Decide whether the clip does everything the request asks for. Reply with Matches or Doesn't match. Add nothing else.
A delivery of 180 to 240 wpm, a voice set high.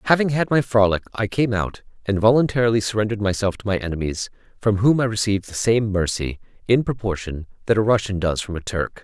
Doesn't match